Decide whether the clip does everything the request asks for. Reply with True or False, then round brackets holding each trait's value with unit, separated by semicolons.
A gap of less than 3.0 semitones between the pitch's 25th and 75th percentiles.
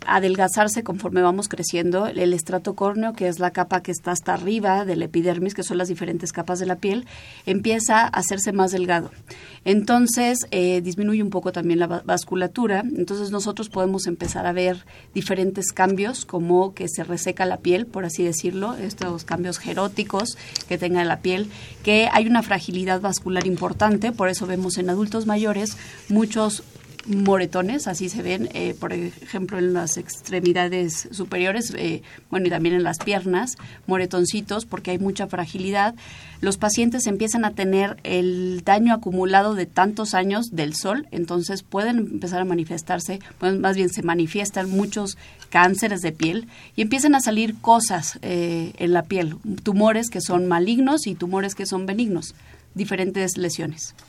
True (2.4 semitones)